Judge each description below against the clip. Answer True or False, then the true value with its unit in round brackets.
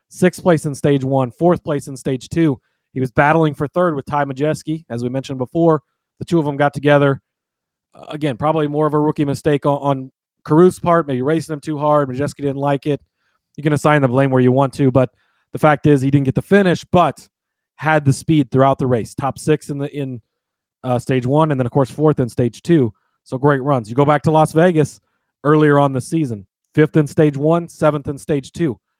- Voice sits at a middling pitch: True (145 Hz)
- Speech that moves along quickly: True (230 wpm)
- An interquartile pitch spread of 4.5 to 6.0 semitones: False (2.5 semitones)